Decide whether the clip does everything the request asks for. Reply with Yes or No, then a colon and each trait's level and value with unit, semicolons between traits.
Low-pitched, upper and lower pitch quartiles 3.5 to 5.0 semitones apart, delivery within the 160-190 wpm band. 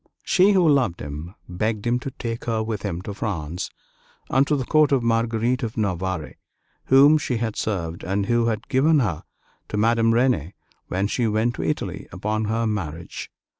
Yes: low, 110 Hz; average, 4.1 semitones; average, 180 wpm